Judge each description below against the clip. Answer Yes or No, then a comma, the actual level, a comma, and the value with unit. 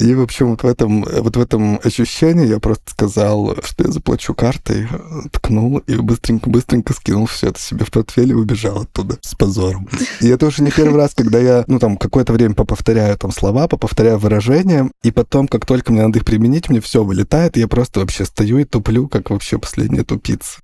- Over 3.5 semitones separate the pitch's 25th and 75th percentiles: No, average, 3.1 semitones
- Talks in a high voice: No, low, 115 Hz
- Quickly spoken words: Yes, fast, 205 wpm